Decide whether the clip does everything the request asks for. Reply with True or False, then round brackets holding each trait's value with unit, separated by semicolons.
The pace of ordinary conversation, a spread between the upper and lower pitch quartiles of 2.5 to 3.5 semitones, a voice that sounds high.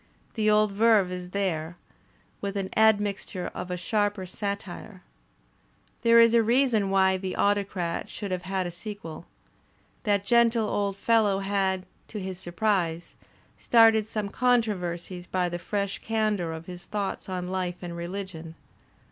True (150 wpm; 2.9 semitones; 195 Hz)